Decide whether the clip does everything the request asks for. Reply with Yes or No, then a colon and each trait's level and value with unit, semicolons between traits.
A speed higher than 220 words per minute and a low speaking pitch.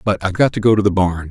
Yes: fast, 370 wpm; low, 100 Hz